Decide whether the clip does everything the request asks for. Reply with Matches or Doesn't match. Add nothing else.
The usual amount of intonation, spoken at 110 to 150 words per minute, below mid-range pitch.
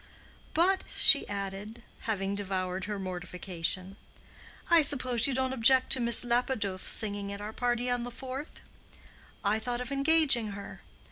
Doesn't match